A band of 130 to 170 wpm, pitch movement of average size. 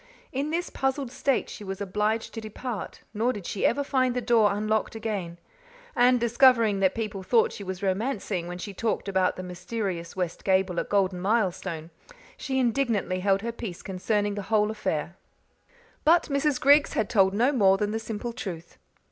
No: average, 180 wpm; average, 4.0 semitones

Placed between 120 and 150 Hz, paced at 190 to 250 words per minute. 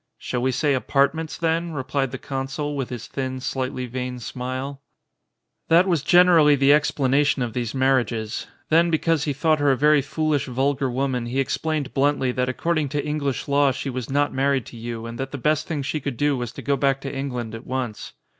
Yes: low, 135 Hz; average, 200 wpm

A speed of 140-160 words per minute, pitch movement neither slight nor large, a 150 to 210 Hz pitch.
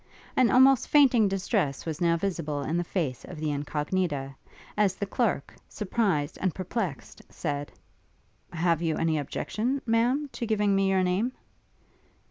No: average, 145 wpm; wide, 5.8 semitones; medium, 185 Hz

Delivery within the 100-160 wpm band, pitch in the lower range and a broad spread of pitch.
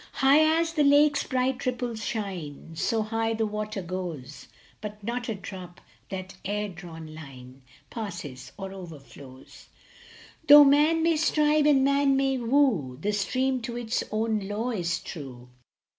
No: average, 150 wpm; high, 215 Hz; wide, 7.3 semitones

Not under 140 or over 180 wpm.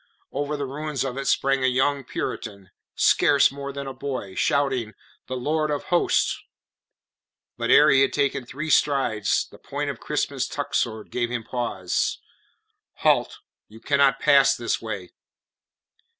Yes: average, 150 wpm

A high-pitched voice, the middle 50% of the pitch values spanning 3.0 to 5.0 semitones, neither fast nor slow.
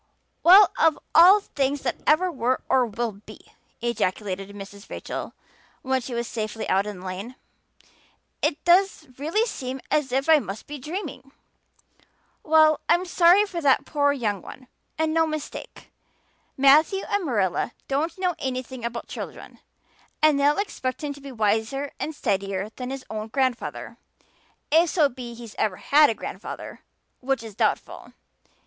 No: very high, 270 Hz; wide, 5.6 semitones; average, 155 wpm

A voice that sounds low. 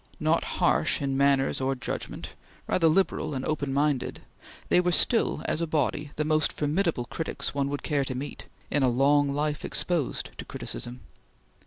No: medium, 145 Hz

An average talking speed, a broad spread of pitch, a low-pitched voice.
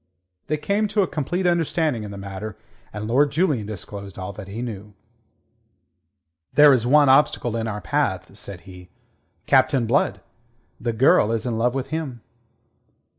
Yes: average, 160 wpm; wide, 6.0 semitones; low, 120 Hz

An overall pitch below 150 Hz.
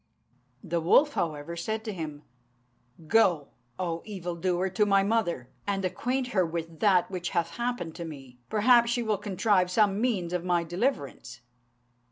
No: medium, 185 Hz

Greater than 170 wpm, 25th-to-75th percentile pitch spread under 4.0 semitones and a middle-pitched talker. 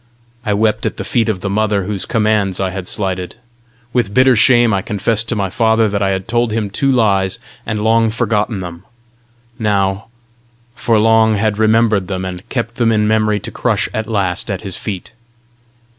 No: average, 190 wpm; narrow, 2.5 semitones; low, 105 Hz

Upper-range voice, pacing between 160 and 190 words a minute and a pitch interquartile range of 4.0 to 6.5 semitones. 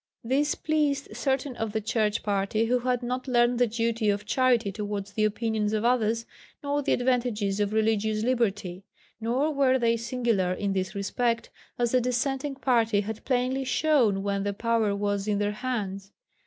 No: high, 230 Hz; average, 170 wpm; average, 3.4 semitones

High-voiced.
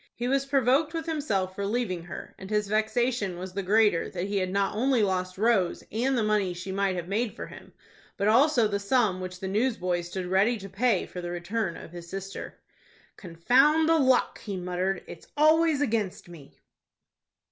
Yes: high, 200 Hz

